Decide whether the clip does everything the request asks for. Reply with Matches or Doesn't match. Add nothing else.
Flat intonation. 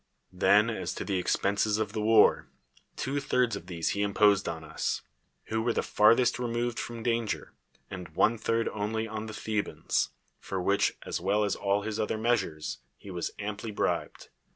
Matches